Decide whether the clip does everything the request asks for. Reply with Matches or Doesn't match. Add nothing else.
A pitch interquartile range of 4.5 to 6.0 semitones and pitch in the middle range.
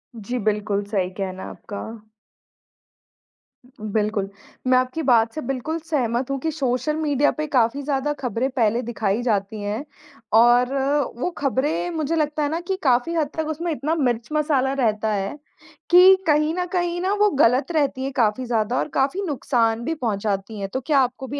Doesn't match